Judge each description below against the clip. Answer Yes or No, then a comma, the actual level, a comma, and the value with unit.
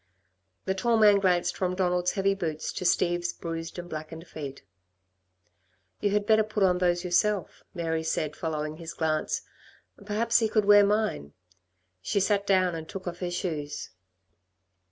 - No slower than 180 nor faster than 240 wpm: No, average, 155 wpm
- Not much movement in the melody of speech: No, average, 3.6 semitones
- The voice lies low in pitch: No, medium, 180 Hz